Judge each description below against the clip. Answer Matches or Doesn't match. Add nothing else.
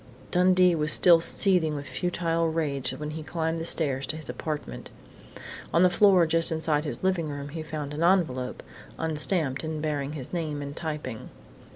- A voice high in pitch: Doesn't match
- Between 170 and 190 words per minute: Matches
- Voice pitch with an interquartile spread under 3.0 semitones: Matches